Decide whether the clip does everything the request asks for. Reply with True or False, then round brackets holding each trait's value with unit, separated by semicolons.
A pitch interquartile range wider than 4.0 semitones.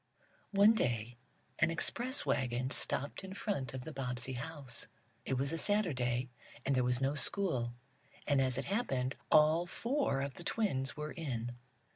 True (5.4 semitones)